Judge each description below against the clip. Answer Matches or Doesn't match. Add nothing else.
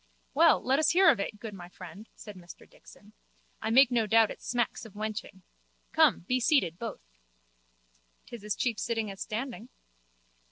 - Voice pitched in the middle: Doesn't match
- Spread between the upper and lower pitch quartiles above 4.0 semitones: Doesn't match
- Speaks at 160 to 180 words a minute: Matches